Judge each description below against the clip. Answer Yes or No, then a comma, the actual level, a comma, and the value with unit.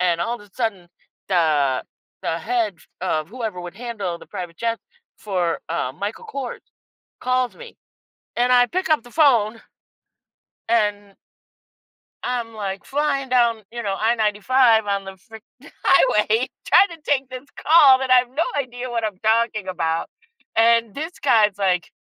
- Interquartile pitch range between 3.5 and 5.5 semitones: Yes, average, 4.3 semitones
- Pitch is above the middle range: Yes, high, 225 Hz